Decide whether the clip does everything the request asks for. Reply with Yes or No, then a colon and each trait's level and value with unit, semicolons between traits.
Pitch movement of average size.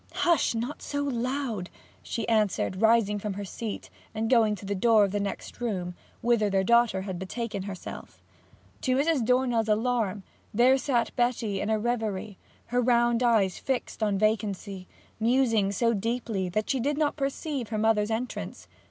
Yes: average, 3.2 semitones